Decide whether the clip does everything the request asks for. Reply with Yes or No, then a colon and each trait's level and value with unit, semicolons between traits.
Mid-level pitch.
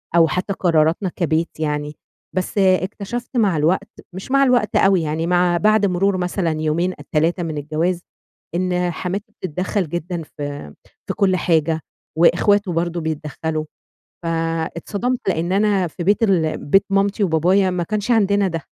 Yes: medium, 180 Hz